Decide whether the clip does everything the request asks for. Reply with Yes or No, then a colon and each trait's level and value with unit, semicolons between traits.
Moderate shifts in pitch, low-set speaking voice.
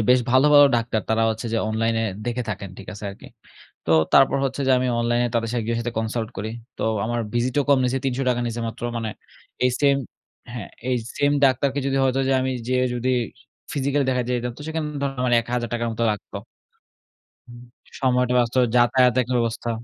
No: narrow, 2.1 semitones; low, 120 Hz